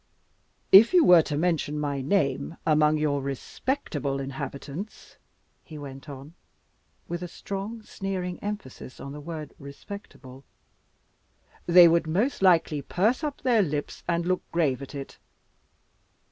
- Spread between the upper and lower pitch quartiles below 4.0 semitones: No, average, 5.3 semitones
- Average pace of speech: No, slow, 130 wpm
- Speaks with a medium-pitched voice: Yes, medium, 160 Hz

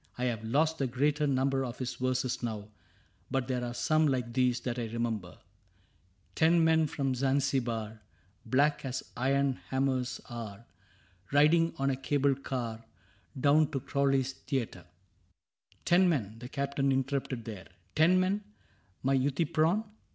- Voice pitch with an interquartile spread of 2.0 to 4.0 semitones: Yes, average, 3.1 semitones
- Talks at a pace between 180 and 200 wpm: No, average, 155 wpm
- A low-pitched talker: Yes, low, 130 Hz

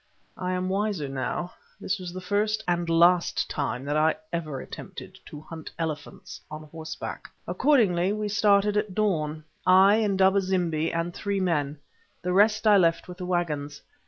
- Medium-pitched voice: Yes, medium, 180 Hz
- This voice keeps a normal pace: Yes, average, 160 wpm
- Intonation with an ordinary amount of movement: Yes, average, 3.9 semitones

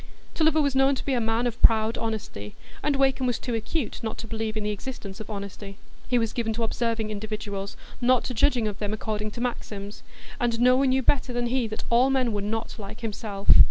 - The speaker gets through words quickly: Yes, fast, 225 wpm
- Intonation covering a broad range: No, average, 2.9 semitones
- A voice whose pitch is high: Yes, high, 225 Hz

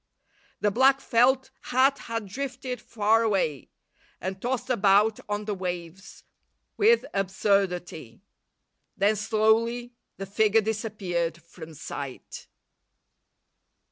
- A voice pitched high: Yes, high, 210 Hz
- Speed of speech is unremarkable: No, slow, 100 wpm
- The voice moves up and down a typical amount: Yes, average, 4.1 semitones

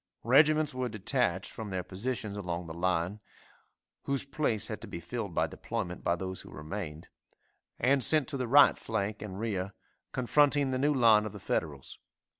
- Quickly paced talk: No, average, 175 wpm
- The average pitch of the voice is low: Yes, low, 105 Hz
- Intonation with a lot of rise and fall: Yes, wide, 5.9 semitones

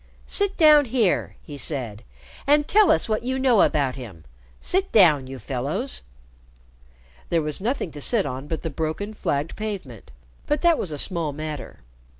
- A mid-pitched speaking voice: Yes, medium, 165 Hz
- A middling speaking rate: Yes, average, 165 wpm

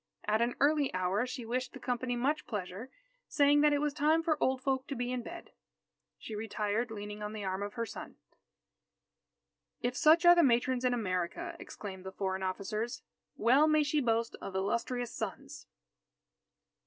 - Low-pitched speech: No, high, 240 Hz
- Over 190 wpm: No, average, 175 wpm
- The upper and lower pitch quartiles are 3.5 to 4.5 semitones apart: No, average, 5.2 semitones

